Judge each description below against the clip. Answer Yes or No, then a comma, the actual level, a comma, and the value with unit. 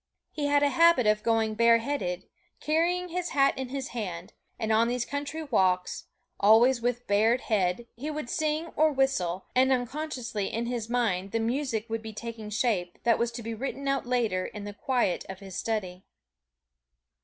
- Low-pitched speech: No, high, 235 Hz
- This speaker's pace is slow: No, average, 180 wpm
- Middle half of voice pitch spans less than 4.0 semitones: No, average, 4.4 semitones